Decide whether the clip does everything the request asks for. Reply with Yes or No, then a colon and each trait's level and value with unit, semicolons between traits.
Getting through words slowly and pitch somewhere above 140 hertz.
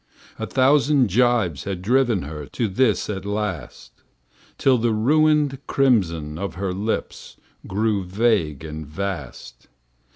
No: slow, 125 wpm; low, 105 Hz